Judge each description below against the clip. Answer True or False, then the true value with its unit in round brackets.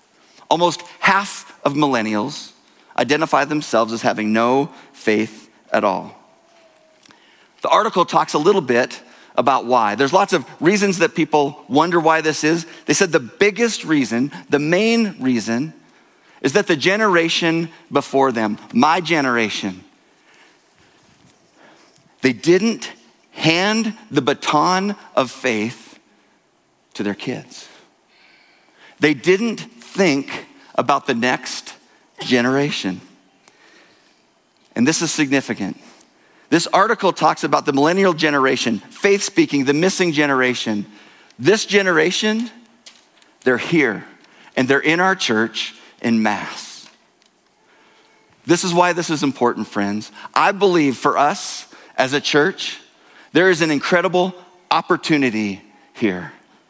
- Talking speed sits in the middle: False (115 wpm)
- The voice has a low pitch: False (160 Hz)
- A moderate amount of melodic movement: False (6.2 semitones)